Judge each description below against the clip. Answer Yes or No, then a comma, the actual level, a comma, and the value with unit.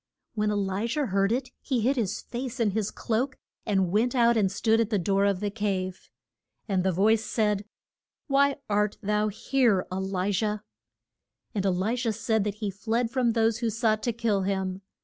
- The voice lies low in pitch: No, high, 210 Hz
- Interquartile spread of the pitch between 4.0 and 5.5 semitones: No, average, 2.8 semitones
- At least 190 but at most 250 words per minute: Yes, average, 200 wpm